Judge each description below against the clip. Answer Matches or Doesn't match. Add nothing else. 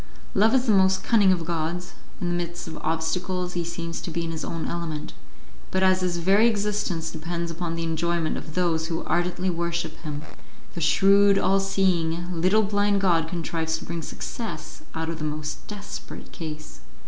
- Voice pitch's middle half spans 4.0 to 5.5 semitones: Doesn't match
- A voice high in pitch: Doesn't match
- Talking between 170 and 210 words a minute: Matches